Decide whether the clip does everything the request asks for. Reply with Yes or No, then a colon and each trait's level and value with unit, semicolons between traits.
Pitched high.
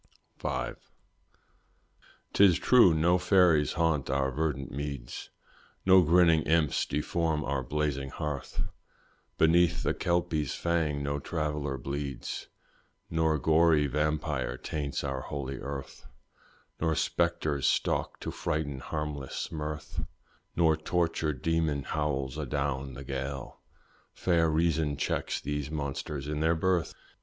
No: very low, 75 Hz